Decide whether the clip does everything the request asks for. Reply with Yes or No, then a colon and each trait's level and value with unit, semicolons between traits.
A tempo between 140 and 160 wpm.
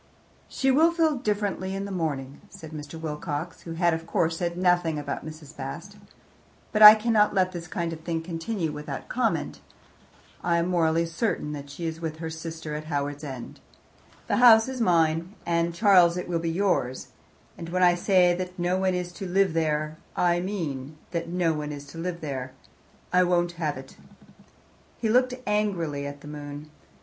No: average, 185 wpm